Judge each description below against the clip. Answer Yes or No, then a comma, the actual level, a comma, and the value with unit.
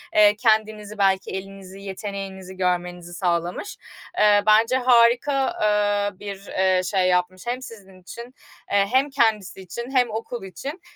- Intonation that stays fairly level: No, average, 3.4 semitones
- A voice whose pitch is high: Yes, high, 205 Hz